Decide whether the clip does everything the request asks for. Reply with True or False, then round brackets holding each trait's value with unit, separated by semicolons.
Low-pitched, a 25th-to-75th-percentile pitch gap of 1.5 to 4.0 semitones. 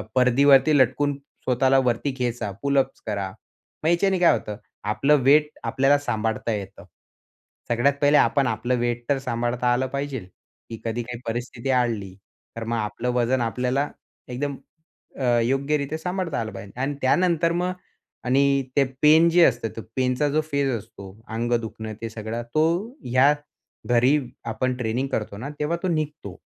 True (130 Hz; 3.6 semitones)